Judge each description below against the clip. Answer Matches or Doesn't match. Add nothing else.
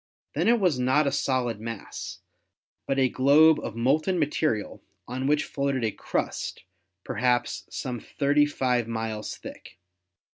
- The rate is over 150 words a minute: Doesn't match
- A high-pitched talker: Doesn't match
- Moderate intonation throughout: Matches